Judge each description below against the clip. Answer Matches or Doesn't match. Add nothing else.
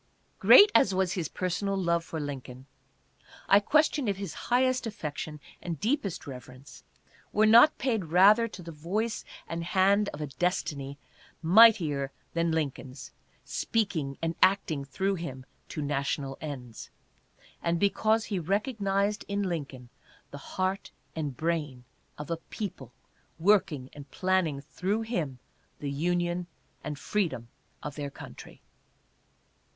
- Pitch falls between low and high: Matches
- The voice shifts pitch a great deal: Matches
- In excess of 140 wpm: Doesn't match